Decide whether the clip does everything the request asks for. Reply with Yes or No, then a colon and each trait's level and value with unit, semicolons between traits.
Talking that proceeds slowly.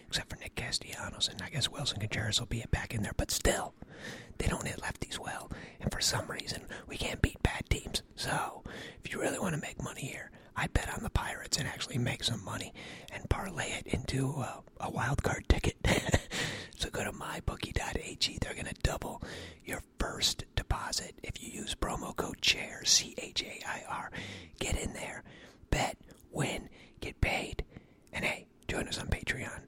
No: average, 185 wpm